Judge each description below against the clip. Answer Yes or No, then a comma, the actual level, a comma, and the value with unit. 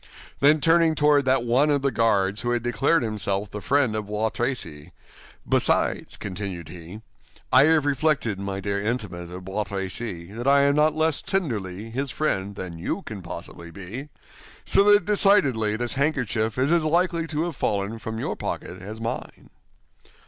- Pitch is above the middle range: No, low, 115 Hz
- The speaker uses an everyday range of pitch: No, wide, 6.5 semitones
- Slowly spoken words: No, average, 170 wpm